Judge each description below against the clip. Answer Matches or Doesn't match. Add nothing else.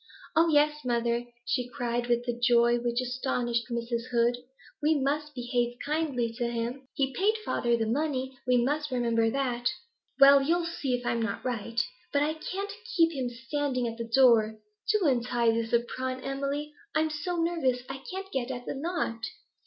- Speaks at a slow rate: Doesn't match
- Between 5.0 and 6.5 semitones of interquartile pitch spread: Doesn't match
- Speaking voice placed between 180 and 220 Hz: Doesn't match